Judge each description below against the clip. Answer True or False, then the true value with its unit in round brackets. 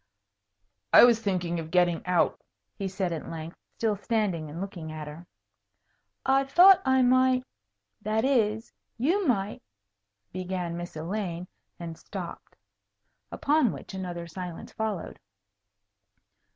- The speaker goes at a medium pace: False (125 wpm)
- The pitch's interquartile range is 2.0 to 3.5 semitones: False (5.2 semitones)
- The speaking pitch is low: False (190 Hz)